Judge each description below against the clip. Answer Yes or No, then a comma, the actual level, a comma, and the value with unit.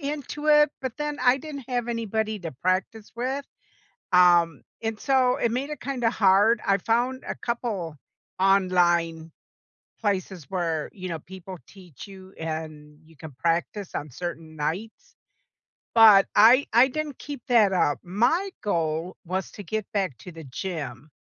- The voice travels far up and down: Yes, wide, 6.2 semitones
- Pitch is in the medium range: No, high, 195 Hz